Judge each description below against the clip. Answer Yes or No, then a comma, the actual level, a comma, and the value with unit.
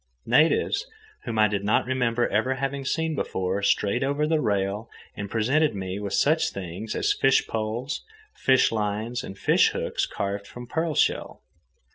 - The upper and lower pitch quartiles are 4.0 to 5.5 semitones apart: Yes, average, 5.0 semitones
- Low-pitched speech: Yes, low, 115 Hz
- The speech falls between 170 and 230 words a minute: No, average, 160 wpm